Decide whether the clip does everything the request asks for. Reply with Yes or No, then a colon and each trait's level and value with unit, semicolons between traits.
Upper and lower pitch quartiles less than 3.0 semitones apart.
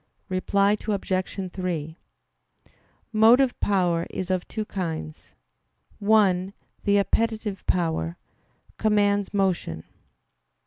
Yes: narrow, 2.6 semitones